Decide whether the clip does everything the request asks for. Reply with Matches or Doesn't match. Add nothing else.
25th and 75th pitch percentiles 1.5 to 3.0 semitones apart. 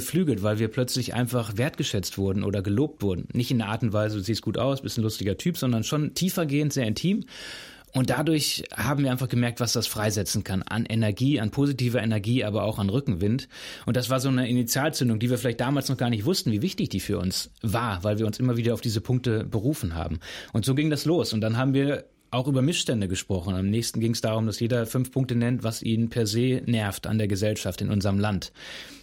Doesn't match